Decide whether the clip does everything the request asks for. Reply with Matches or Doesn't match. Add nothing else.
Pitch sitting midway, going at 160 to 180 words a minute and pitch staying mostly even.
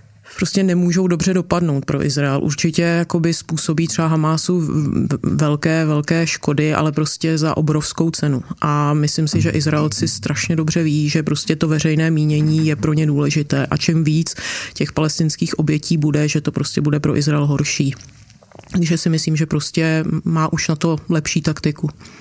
Matches